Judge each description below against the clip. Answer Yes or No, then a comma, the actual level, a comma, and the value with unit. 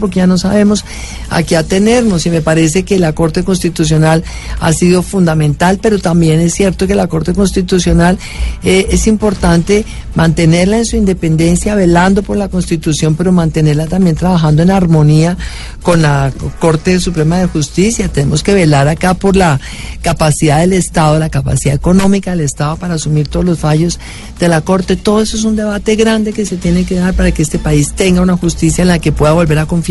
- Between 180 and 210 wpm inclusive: Yes, fast, 190 wpm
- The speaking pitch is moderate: Yes, medium, 175 Hz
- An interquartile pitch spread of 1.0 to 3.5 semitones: Yes, average, 2.9 semitones